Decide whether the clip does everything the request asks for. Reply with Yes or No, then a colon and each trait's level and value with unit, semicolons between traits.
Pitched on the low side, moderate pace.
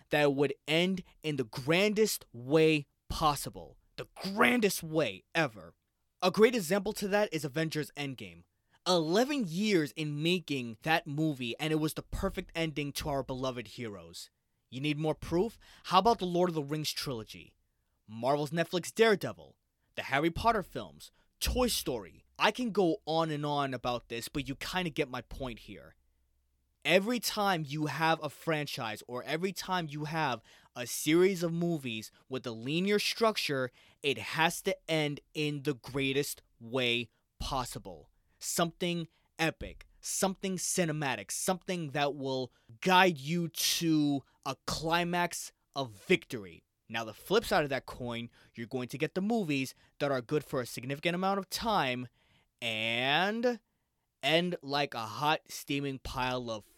No: medium, 150 Hz; average, 155 wpm